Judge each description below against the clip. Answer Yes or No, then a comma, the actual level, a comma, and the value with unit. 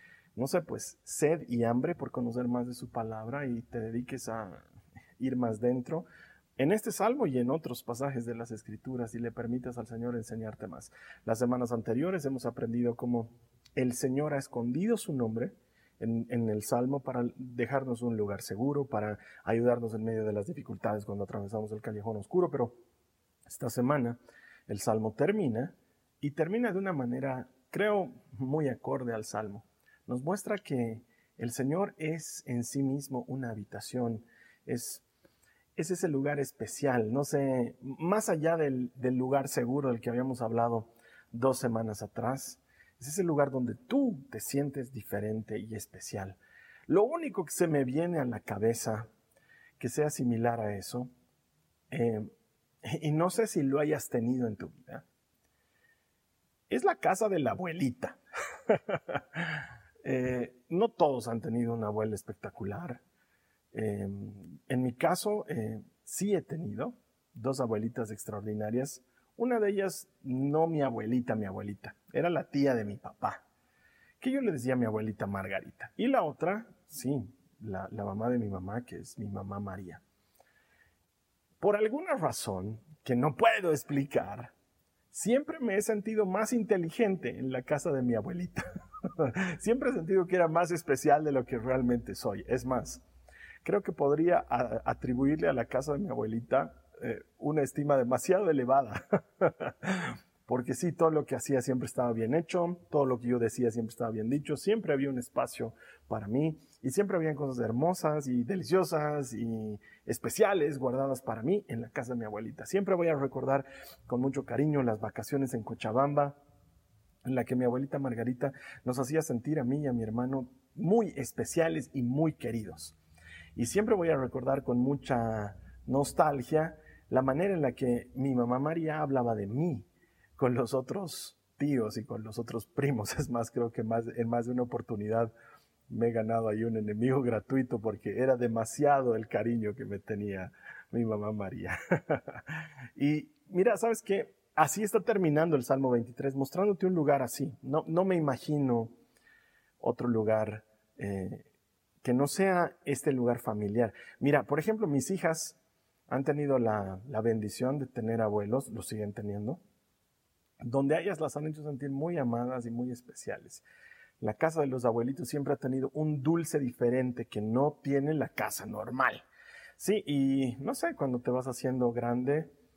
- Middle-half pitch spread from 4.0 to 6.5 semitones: Yes, average, 4.4 semitones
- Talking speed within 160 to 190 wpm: Yes, average, 165 wpm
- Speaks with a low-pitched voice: Yes, low, 125 Hz